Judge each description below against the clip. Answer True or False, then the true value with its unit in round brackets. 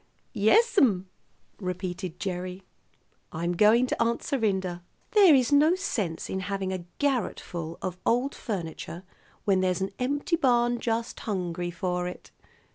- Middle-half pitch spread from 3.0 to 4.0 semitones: False (5.3 semitones)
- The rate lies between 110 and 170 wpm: True (135 wpm)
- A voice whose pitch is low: False (195 Hz)